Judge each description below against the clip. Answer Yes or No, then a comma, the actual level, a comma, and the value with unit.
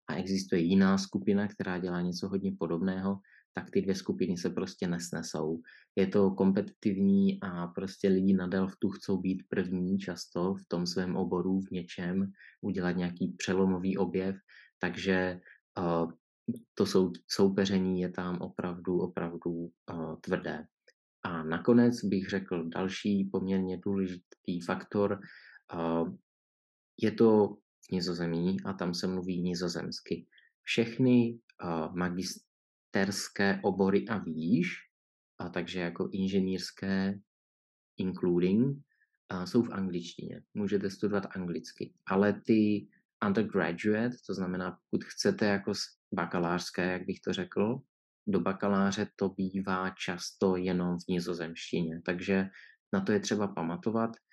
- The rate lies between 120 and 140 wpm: Yes, average, 125 wpm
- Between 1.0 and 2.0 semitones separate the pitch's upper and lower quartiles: Yes, narrow, 1.7 semitones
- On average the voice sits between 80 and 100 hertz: Yes, very low, 95 Hz